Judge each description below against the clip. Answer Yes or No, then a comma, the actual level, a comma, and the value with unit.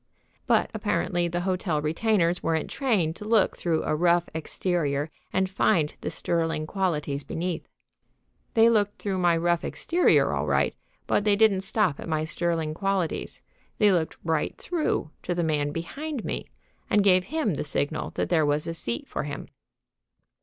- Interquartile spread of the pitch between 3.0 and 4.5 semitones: Yes, average, 3.9 semitones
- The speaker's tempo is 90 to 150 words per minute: No, average, 165 wpm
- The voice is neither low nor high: Yes, medium, 175 Hz